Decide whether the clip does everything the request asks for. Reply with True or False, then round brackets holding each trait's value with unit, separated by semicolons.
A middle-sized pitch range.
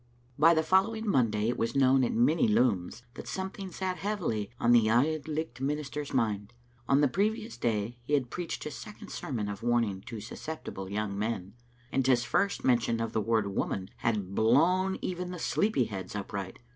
False (6.9 semitones)